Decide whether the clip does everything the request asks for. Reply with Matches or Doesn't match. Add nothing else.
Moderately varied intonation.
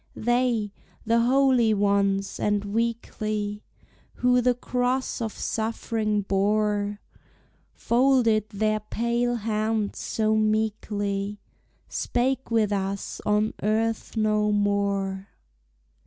Doesn't match